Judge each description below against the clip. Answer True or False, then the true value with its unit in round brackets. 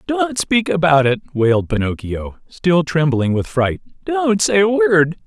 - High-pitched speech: False (165 Hz)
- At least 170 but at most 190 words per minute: False (160 wpm)